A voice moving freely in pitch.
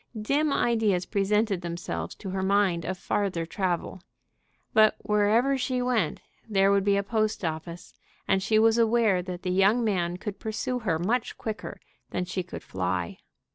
No: average, 3.5 semitones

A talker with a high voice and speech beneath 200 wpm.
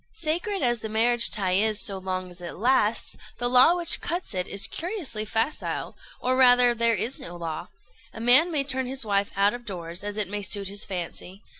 No: high, 220 Hz; fast, 205 wpm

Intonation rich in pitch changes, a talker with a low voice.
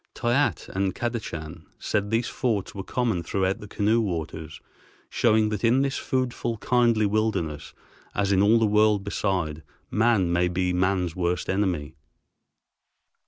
No: average, 4.1 semitones; low, 100 Hz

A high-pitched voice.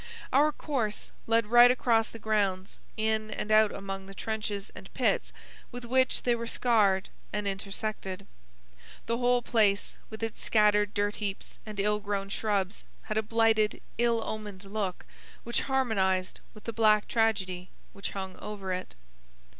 Yes: high, 215 Hz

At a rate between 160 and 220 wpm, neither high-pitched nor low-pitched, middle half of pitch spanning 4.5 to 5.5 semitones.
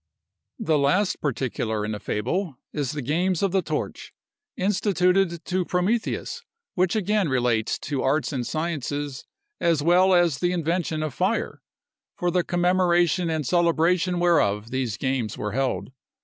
No: average, 145 wpm; medium, 170 Hz; average, 5.1 semitones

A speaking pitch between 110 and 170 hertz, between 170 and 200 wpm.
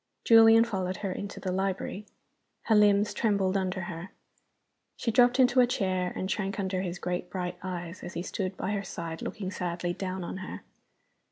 No: high, 190 Hz; average, 180 wpm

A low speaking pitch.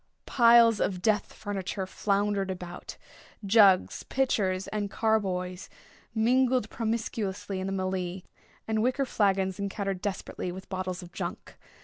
No: high, 200 Hz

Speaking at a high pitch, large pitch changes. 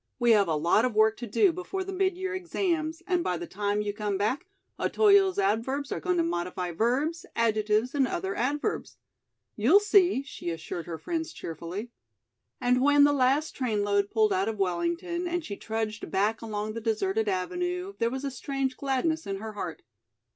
Yes: high, 235 Hz; wide, 7.9 semitones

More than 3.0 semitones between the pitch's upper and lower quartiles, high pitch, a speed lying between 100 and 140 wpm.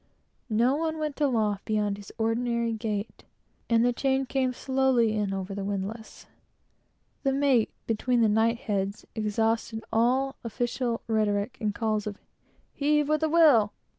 No: average, 3.8 semitones; high, 230 Hz; average, 150 wpm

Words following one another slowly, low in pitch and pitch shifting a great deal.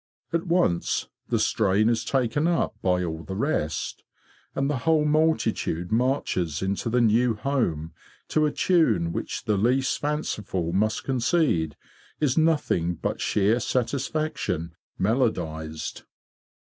Yes: slow, 125 wpm; low, 115 Hz; wide, 8.3 semitones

